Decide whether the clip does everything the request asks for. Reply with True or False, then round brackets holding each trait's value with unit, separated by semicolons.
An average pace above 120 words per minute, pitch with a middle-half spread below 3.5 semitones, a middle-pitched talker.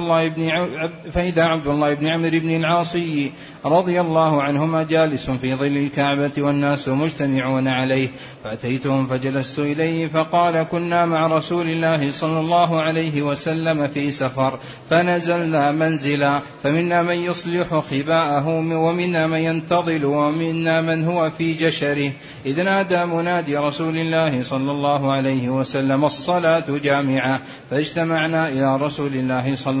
True (130 wpm; 2.7 semitones; 155 Hz)